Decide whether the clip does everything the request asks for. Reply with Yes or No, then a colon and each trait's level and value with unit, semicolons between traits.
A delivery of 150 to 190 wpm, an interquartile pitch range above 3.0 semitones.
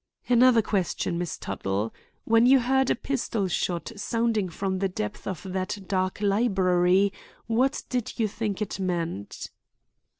No: average, 140 wpm; average, 3.9 semitones